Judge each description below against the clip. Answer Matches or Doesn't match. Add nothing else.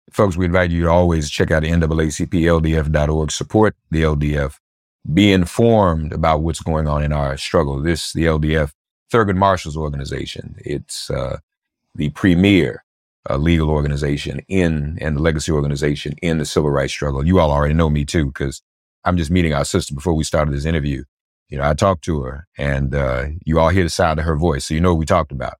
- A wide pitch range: Doesn't match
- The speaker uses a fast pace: Doesn't match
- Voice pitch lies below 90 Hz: Matches